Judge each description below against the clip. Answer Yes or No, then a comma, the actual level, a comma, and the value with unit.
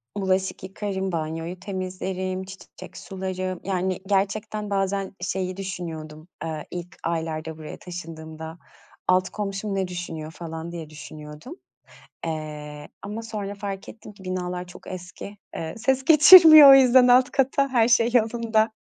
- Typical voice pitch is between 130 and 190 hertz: Yes, medium, 185 Hz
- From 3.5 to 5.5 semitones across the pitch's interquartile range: Yes, average, 4.0 semitones